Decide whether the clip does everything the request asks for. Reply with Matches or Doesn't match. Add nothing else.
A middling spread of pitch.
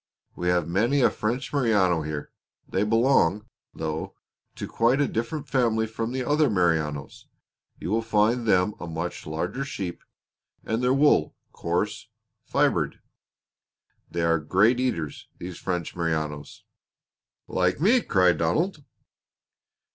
Doesn't match